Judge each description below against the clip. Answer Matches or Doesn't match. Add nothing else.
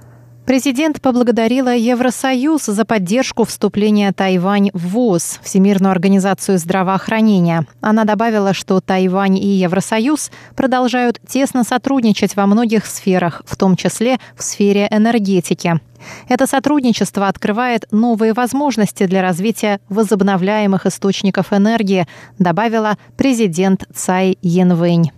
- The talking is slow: Matches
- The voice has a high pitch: Matches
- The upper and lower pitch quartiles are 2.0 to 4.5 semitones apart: Matches